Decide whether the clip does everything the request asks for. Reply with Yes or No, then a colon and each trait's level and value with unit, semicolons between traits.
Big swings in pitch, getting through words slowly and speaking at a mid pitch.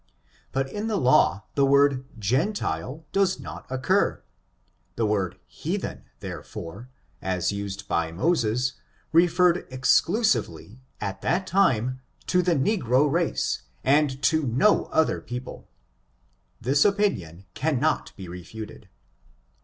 No: wide, 7.7 semitones; slow, 115 wpm; low, 130 Hz